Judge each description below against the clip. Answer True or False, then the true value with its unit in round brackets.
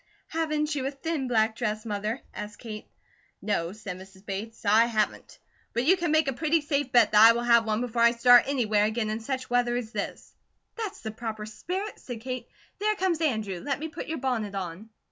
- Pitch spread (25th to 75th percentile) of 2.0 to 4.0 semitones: False (4.8 semitones)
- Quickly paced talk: True (210 wpm)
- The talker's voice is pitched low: False (235 Hz)